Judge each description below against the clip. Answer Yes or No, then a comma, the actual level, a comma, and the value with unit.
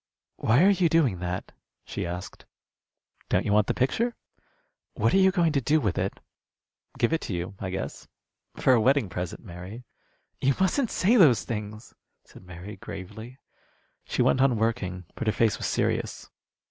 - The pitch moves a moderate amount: No, wide, 8.2 semitones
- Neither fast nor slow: Yes, average, 170 wpm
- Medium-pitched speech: No, low, 115 Hz